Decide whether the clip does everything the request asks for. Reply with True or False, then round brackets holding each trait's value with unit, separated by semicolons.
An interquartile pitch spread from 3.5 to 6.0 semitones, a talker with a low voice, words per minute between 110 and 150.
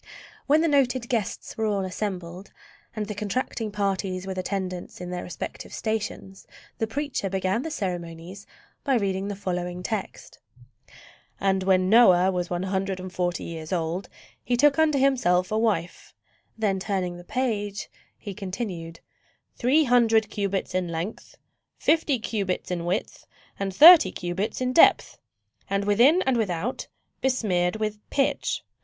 False (4.0 semitones; 200 Hz; 145 wpm)